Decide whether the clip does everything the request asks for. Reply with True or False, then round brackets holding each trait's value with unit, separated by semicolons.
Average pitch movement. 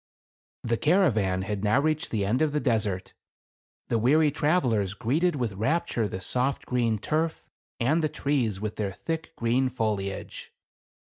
False (6.1 semitones)